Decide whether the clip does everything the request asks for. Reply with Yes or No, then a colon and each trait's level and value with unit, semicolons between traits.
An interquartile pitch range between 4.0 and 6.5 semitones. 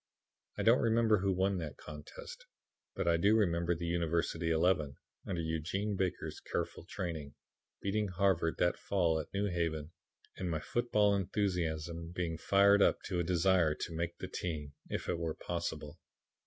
No: average, 3.2 semitones